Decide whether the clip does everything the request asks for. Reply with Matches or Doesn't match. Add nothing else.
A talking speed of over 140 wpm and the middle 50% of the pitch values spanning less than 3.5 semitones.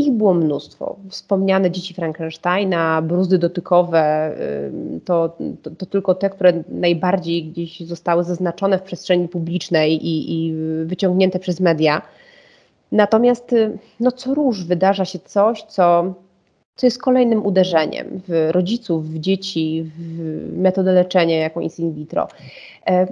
Doesn't match